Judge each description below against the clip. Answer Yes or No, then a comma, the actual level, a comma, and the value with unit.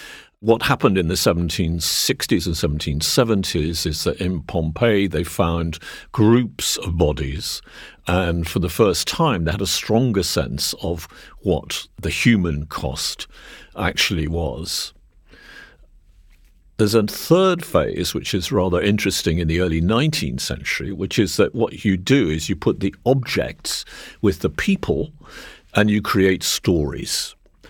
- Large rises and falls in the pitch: No, average, 4.5 semitones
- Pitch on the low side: Yes, very low, 90 Hz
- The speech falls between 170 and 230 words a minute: No, average, 140 wpm